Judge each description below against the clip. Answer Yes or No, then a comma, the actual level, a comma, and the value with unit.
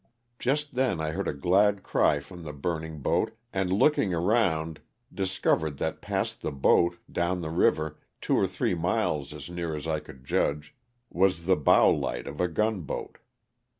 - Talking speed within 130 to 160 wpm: No, average, 175 wpm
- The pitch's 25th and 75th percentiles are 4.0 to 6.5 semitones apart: No, average, 3.6 semitones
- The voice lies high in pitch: No, very low, 85 Hz